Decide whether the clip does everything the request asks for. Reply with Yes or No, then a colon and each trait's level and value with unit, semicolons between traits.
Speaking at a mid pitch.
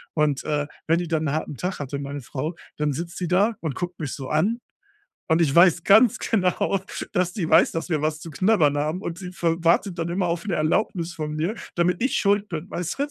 Yes: medium, 170 Hz